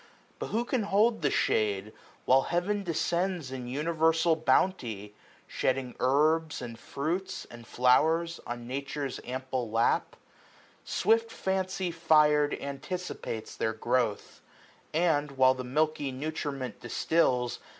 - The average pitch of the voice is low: No, medium, 145 Hz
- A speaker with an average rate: No, slow, 120 wpm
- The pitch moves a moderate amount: Yes, average, 5.0 semitones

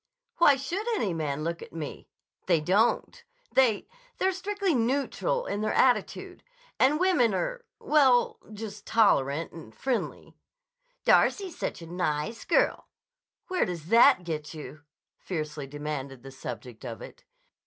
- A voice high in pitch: Yes, high, 205 Hz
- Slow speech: Yes, slow, 125 wpm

